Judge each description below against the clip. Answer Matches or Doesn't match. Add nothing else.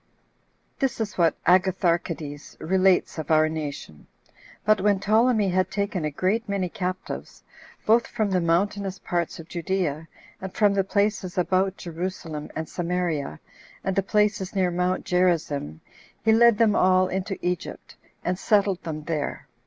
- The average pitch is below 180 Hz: Doesn't match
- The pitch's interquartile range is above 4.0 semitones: Doesn't match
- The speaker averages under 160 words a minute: Matches